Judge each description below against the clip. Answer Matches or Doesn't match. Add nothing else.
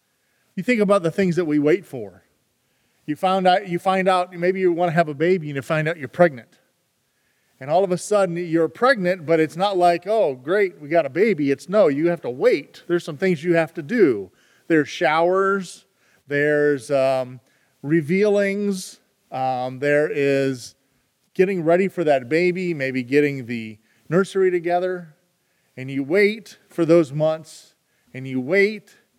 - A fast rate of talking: Doesn't match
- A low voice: Doesn't match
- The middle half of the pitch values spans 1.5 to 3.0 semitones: Doesn't match